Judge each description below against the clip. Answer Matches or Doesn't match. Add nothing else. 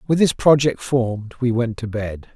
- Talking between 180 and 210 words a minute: Matches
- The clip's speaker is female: Doesn't match